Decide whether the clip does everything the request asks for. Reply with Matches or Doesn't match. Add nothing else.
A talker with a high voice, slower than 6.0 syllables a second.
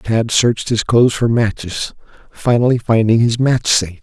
Doesn't match